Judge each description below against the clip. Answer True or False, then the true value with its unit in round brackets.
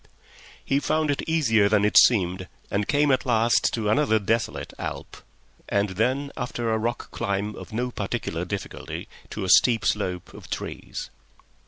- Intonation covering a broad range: False (3.8 semitones)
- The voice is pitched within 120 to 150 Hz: False (110 Hz)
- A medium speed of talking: True (160 wpm)